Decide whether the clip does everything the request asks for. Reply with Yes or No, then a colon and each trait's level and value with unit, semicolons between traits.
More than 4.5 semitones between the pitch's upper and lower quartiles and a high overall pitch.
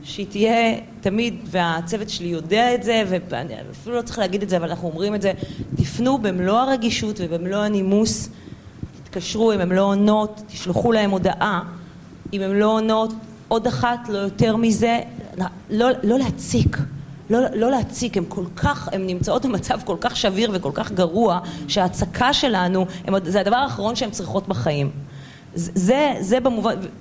No: average, 4.1 semitones; high, 200 Hz